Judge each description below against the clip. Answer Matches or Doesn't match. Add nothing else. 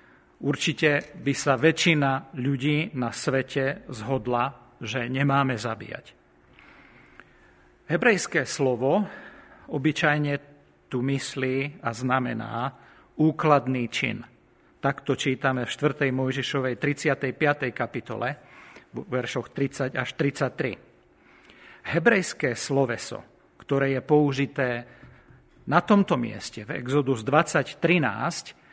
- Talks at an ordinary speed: Doesn't match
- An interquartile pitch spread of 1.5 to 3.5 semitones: Matches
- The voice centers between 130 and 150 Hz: Matches